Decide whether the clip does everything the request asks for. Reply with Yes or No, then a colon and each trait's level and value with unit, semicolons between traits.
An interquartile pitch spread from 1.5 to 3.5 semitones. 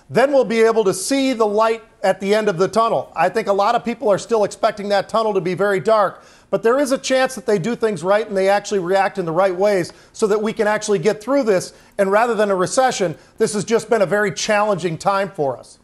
Yes: narrow, 2.5 semitones